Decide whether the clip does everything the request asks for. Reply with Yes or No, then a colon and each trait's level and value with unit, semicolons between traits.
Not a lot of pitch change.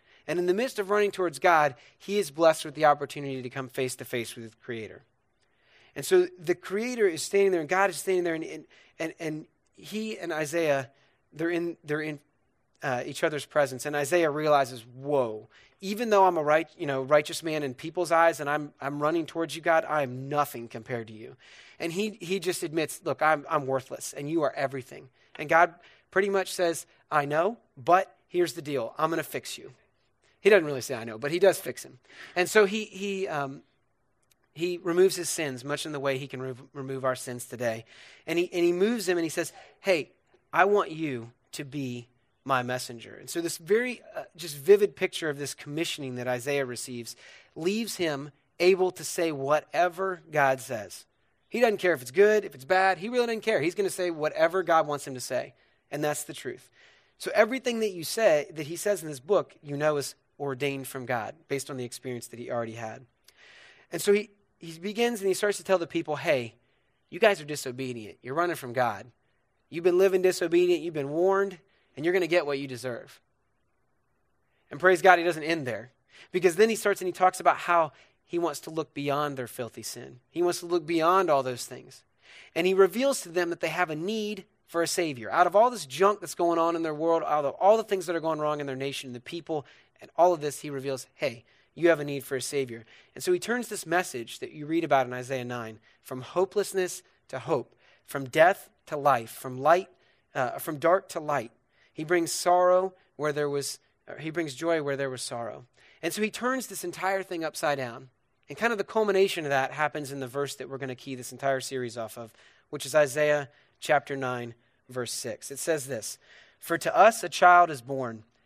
No: average, 5.1 semitones